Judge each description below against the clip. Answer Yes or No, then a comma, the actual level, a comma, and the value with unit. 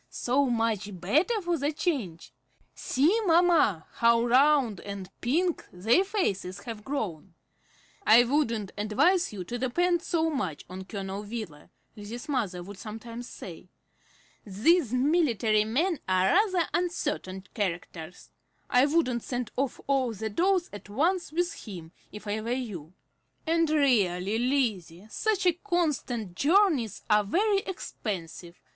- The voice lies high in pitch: Yes, high, 235 Hz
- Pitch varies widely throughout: Yes, wide, 8.1 semitones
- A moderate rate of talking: No, slow, 130 wpm